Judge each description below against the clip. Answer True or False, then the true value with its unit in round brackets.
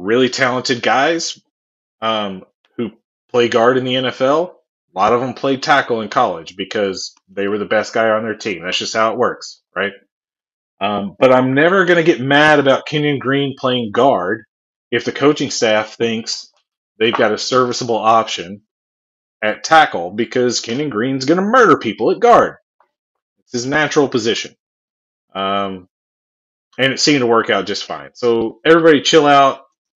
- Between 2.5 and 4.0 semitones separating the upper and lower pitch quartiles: False (4.7 semitones)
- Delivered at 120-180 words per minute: True (170 wpm)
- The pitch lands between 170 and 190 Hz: False (125 Hz)